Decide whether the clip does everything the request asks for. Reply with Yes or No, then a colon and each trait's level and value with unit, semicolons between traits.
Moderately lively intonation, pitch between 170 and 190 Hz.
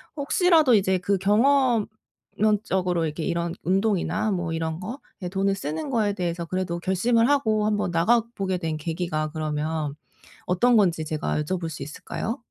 Yes: average, 4.7 semitones; medium, 185 Hz